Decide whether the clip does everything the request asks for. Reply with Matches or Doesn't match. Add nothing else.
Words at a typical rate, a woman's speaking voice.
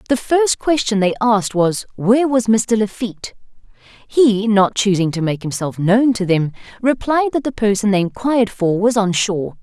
Matches